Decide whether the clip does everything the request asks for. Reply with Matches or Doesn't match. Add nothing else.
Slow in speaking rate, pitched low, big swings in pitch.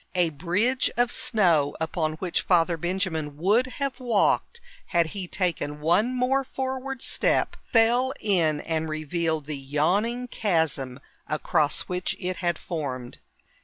Doesn't match